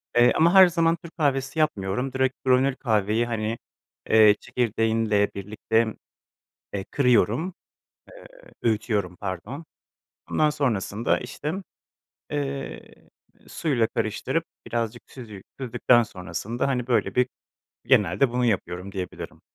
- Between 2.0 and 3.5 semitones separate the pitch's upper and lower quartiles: No, average, 4.3 semitones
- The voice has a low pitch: Yes, low, 120 Hz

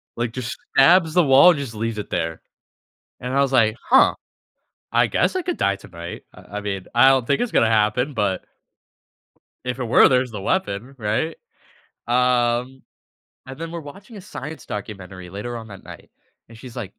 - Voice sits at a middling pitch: No, low, 120 Hz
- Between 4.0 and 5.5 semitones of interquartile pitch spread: Yes, average, 4.7 semitones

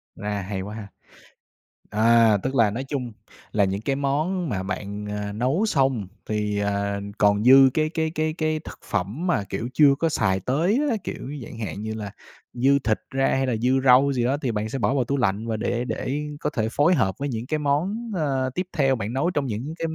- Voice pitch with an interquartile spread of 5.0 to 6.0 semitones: Yes, wide, 5.4 semitones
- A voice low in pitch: Yes, low, 125 Hz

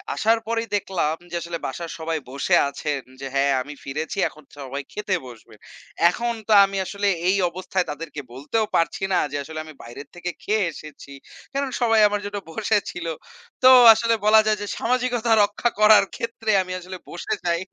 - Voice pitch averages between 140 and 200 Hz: Yes, medium, 185 Hz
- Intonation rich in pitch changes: Yes, wide, 6.1 semitones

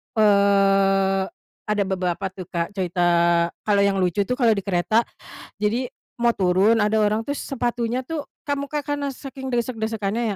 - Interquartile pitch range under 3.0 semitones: No, average, 3.6 semitones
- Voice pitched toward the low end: No, high, 210 Hz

